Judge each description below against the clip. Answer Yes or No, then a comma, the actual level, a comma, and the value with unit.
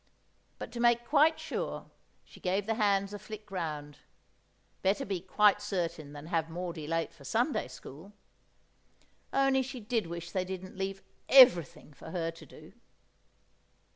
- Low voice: No, high, 190 Hz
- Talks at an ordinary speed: Yes, average, 150 wpm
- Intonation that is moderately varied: Yes, average, 4.6 semitones